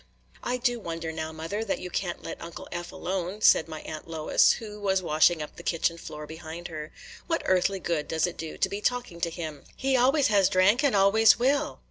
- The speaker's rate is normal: No, fast, 215 wpm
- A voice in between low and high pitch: Yes, medium, 180 Hz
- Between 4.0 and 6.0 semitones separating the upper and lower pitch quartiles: Yes, average, 4.6 semitones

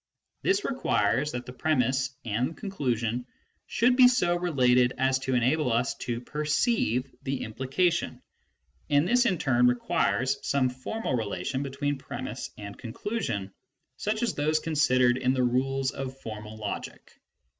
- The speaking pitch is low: Yes, low, 130 Hz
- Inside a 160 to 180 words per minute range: No, average, 140 wpm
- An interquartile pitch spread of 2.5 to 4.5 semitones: Yes, average, 4.0 semitones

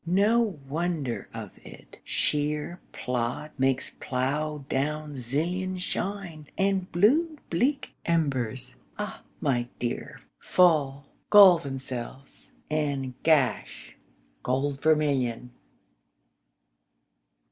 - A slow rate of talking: Yes, slow, 85 wpm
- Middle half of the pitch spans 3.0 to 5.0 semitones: Yes, average, 4.7 semitones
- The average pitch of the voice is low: No, medium, 150 Hz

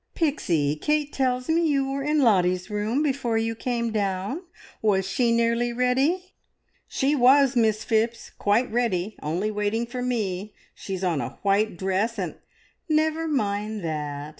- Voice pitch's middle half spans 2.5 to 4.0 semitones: No, average, 5.3 semitones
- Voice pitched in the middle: No, high, 230 Hz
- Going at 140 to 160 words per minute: Yes, average, 155 wpm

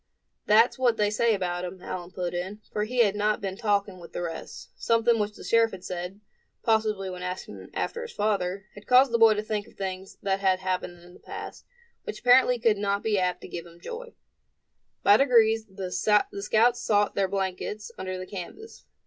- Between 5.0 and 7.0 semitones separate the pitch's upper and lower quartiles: No, average, 3.3 semitones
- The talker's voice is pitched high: Yes, high, 205 Hz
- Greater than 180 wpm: Yes, average, 200 wpm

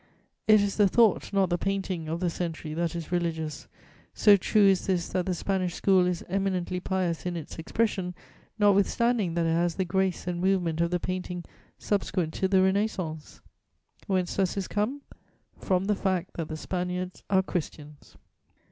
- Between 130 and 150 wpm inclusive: No, average, 175 wpm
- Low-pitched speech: No, medium, 185 Hz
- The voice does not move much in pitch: Yes, narrow, 2.3 semitones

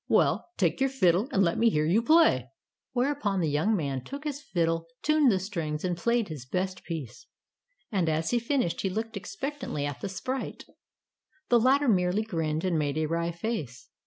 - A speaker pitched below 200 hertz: Yes, medium, 185 Hz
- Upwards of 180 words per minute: Yes, average, 190 wpm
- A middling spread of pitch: No, wide, 6.6 semitones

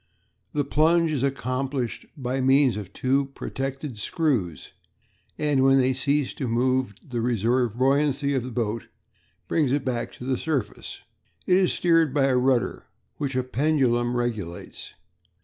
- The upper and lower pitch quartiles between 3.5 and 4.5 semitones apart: No, average, 2.7 semitones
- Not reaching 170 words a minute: Yes, average, 150 wpm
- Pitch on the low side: Yes, low, 130 Hz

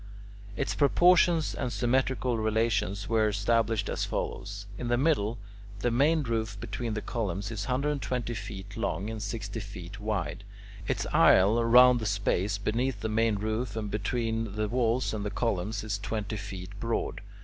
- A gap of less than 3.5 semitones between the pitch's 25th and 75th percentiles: Yes, average, 2.8 semitones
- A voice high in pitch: No, low, 110 Hz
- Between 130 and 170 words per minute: Yes, average, 160 wpm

